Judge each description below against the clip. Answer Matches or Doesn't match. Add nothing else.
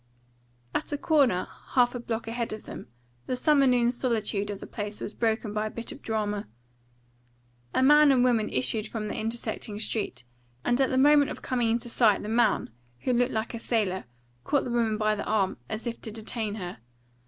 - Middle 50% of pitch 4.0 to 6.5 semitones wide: Doesn't match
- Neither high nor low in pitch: Doesn't match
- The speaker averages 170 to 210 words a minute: Matches